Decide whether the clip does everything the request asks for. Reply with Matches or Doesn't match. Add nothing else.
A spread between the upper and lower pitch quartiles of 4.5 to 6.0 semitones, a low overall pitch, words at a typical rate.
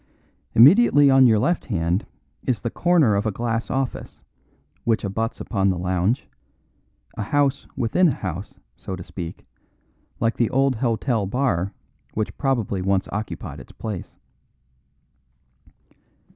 Doesn't match